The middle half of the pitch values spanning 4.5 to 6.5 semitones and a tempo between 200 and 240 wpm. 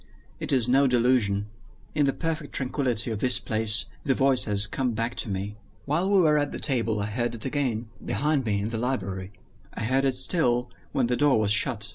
No: average, 4.0 semitones; fast, 205 wpm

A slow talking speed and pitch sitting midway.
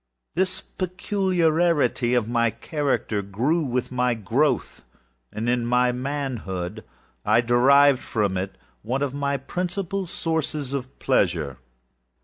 No: slow, 115 wpm; low, 130 Hz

